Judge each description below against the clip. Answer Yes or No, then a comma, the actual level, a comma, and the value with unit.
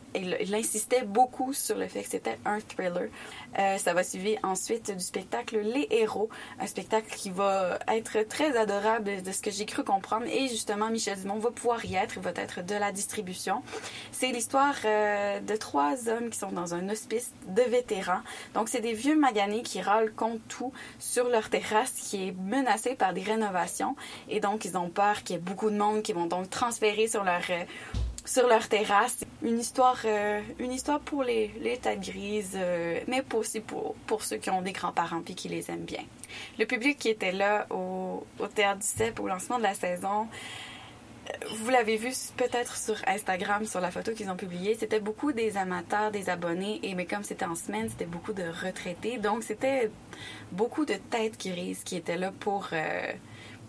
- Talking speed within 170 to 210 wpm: Yes, average, 200 wpm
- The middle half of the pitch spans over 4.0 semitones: No, average, 3.7 semitones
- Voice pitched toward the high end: Yes, high, 215 Hz